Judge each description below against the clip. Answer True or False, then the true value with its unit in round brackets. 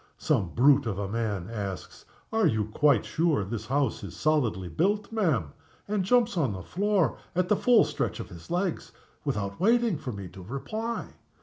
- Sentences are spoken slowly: False (180 wpm)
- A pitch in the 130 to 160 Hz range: True (140 Hz)